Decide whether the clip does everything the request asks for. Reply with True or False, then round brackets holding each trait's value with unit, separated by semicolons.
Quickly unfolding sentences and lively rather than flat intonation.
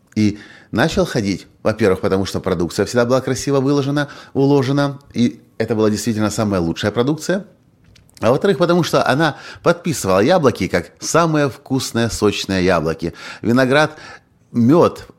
False (130 wpm; 5.8 semitones)